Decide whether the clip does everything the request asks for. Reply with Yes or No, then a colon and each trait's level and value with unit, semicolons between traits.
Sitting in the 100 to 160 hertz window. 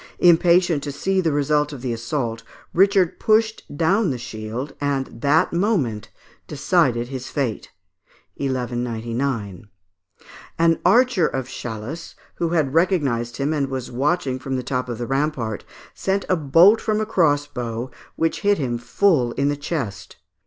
Yes: medium, 140 Hz